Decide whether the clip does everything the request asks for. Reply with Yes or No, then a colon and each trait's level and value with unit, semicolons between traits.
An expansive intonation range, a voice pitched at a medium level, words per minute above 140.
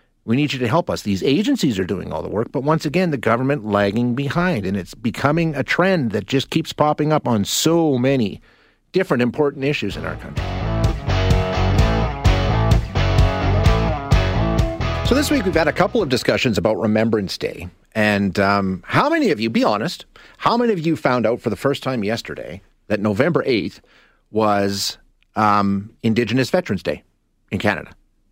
No: wide, 5.7 semitones; low, 110 Hz; average, 170 wpm